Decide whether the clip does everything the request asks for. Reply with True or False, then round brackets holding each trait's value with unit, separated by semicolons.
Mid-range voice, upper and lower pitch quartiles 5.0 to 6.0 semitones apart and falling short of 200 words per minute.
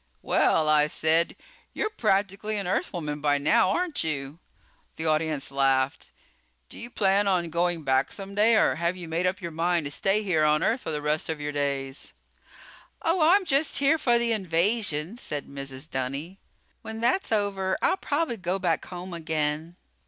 True (170 Hz; 5.6 semitones; 175 wpm)